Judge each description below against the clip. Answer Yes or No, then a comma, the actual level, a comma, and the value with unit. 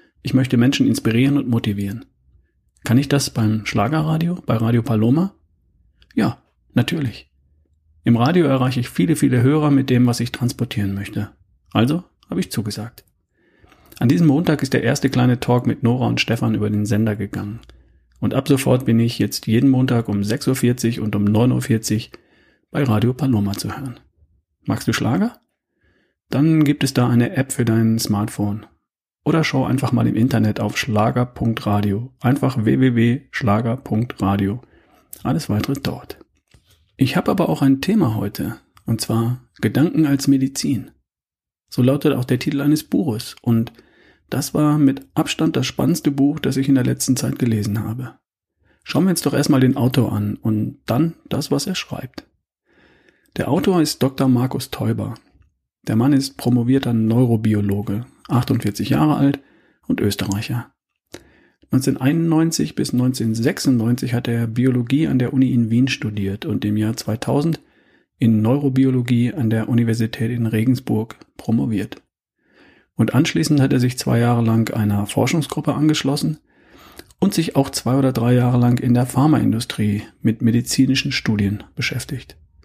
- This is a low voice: Yes, low, 120 Hz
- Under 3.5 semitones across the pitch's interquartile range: No, average, 3.9 semitones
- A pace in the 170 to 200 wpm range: No, average, 150 wpm